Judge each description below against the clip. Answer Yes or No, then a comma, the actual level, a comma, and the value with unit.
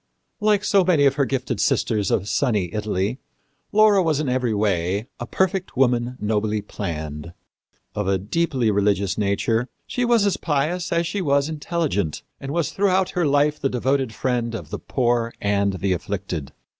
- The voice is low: Yes, low, 125 Hz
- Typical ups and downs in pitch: No, wide, 7.5 semitones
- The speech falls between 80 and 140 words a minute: No, average, 170 wpm